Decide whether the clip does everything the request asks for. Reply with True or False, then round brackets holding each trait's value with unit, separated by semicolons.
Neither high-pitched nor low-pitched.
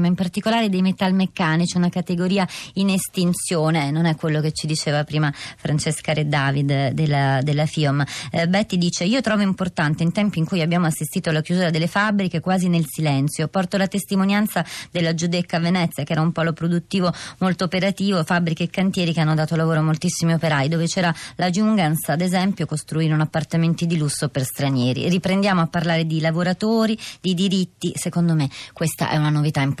True (170 Hz)